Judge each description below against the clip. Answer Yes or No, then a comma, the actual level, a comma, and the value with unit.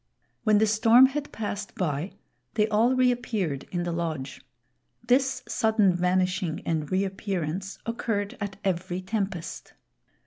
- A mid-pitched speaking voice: No, high, 195 Hz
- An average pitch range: Yes, average, 3.9 semitones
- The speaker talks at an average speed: No, slow, 125 wpm